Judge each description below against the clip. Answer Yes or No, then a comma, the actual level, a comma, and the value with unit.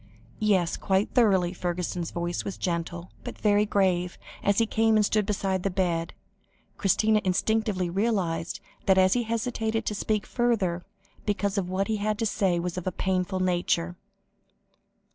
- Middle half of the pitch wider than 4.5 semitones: No, average, 3.1 semitones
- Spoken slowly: No, average, 155 wpm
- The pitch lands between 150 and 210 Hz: Yes, high, 190 Hz